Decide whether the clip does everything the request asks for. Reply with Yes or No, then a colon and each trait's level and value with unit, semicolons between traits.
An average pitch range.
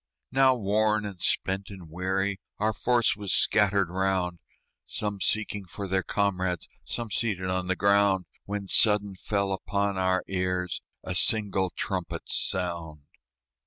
No: narrow, 1.8 semitones